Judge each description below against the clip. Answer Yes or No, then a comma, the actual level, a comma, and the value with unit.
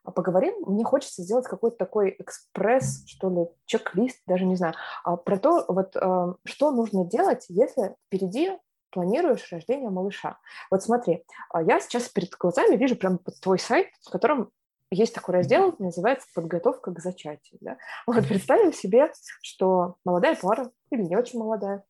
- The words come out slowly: No, average, 150 wpm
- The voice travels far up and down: No, average, 4.7 semitones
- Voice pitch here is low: No, high, 190 Hz